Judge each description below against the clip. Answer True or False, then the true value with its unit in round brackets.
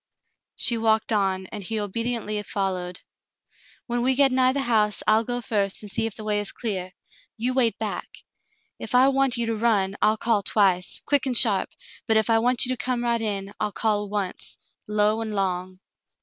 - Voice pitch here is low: False (220 Hz)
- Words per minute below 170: False (195 wpm)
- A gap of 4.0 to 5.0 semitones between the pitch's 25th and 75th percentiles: False (3.0 semitones)